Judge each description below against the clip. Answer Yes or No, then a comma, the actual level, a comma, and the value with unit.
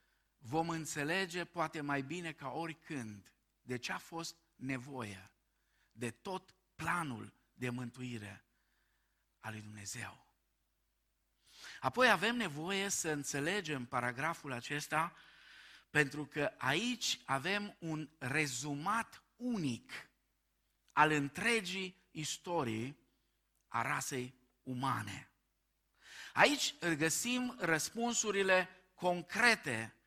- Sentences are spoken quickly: No, slow, 90 wpm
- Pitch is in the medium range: Yes, medium, 155 Hz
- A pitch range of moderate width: No, wide, 6.5 semitones